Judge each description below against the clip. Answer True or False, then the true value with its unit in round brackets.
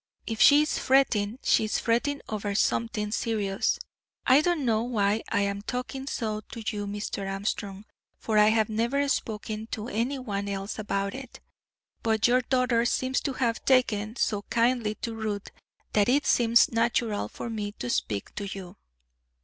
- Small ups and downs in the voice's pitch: False (3.1 semitones)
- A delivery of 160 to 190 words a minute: True (165 wpm)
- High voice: True (220 Hz)